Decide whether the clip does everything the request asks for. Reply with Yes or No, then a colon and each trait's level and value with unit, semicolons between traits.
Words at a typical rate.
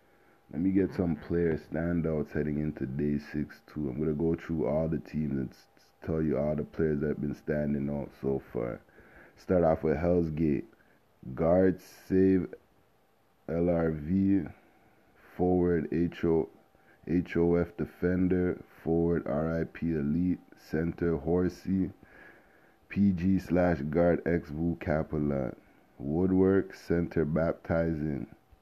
No: slow, 115 wpm